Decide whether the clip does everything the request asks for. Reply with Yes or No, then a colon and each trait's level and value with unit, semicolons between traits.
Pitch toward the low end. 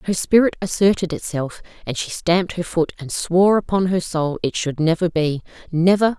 No: medium, 175 Hz